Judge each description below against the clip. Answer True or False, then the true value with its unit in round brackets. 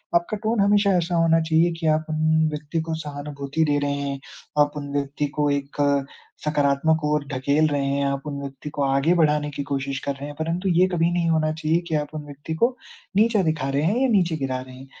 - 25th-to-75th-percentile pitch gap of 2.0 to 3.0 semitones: True (2.7 semitones)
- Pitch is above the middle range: False (150 Hz)